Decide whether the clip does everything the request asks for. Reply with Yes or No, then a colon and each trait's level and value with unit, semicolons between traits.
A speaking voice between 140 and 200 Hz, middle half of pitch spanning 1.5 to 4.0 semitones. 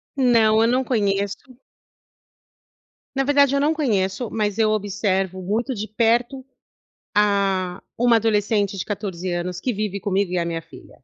No: high, 210 Hz; average, 3.5 semitones